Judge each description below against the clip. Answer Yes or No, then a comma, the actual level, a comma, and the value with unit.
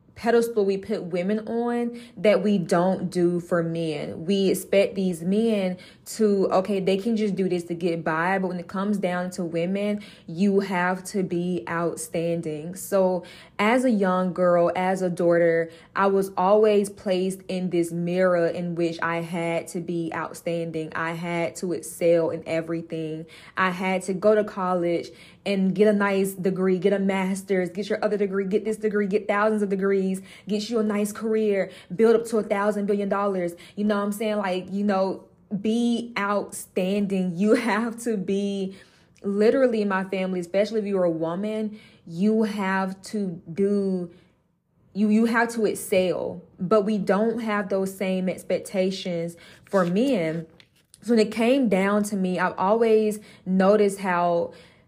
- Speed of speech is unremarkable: Yes, average, 170 wpm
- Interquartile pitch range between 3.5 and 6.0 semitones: No, average, 3.0 semitones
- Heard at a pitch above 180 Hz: Yes, high, 190 Hz